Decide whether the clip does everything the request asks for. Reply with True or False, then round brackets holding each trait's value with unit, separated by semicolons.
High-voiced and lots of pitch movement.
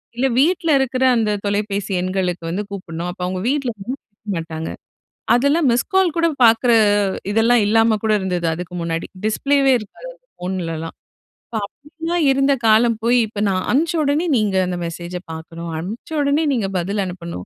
True (215 Hz; 6.9 semitones)